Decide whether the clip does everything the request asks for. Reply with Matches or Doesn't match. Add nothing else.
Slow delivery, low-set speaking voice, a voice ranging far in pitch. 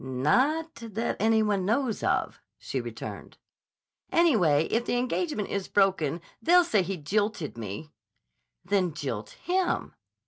Doesn't match